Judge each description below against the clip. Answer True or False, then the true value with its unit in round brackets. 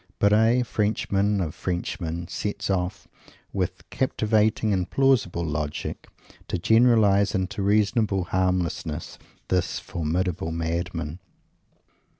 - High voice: False (95 Hz)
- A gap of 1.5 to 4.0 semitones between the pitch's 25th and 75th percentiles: True (3.6 semitones)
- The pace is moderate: False (95 wpm)